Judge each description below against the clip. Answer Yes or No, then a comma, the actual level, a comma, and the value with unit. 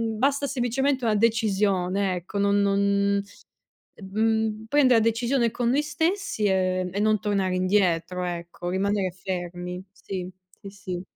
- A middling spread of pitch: Yes, average, 3.6 semitones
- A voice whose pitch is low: No, high, 200 Hz